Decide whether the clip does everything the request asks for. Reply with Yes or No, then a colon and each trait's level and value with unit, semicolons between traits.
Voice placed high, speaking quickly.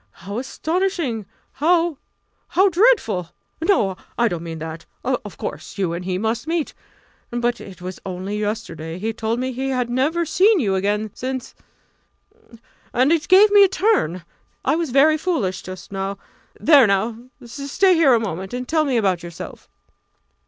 No: high, 240 Hz; average, 160 wpm